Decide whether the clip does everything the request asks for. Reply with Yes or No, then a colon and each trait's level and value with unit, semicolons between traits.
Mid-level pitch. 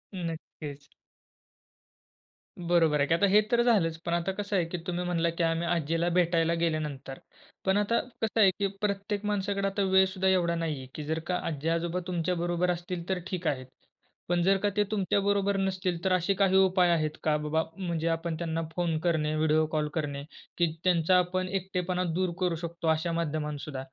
Yes: medium, 175 Hz